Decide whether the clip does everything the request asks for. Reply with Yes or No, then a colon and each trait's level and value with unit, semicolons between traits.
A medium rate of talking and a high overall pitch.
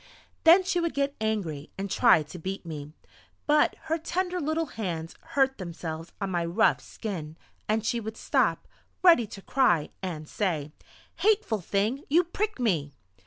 Yes: average, 160 wpm; high, 215 Hz